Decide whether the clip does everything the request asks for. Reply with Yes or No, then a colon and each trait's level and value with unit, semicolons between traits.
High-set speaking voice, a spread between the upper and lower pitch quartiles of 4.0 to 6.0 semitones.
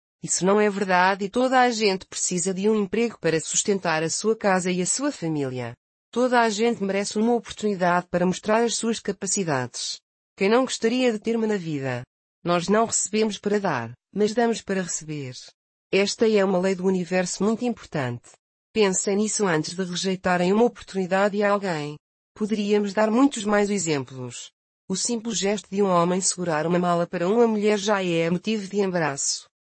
No: high, 195 Hz; average, 3.5 semitones